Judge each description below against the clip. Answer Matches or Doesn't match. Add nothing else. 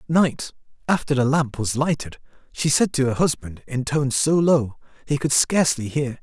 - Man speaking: Matches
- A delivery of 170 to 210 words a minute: Matches